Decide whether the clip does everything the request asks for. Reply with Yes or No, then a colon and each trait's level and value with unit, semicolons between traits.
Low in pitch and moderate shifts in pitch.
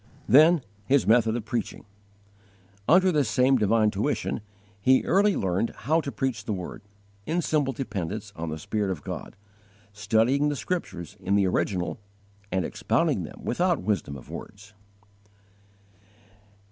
No: low, 115 Hz; wide, 6.1 semitones